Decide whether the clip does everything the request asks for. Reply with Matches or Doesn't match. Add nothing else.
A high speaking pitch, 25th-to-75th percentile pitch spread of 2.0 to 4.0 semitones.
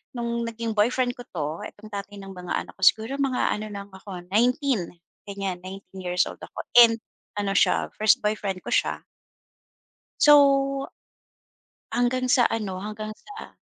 Matches